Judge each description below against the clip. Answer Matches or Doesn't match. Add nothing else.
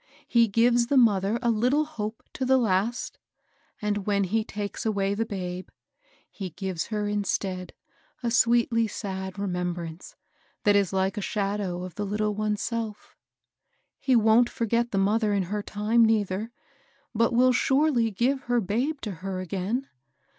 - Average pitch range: Matches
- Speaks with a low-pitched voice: Doesn't match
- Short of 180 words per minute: Matches